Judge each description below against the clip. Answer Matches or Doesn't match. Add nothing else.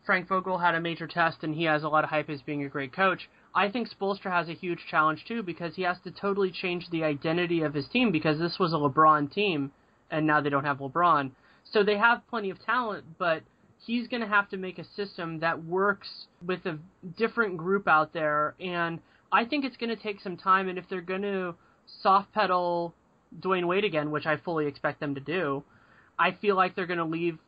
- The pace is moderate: Doesn't match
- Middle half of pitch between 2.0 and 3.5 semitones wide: Doesn't match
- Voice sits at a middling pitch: Matches